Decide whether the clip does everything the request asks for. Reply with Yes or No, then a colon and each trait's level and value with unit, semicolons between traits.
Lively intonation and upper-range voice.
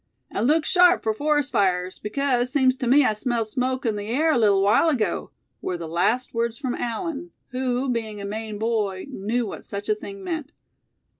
No: average, 4.2 semitones; high, 235 Hz